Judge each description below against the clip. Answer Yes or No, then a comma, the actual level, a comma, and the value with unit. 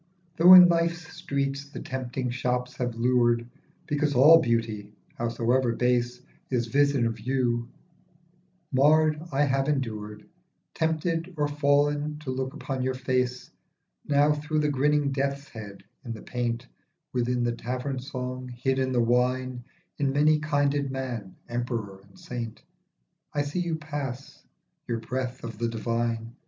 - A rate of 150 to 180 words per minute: No, average, 140 wpm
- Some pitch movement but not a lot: Yes, average, 3.3 semitones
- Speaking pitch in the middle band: No, low, 130 Hz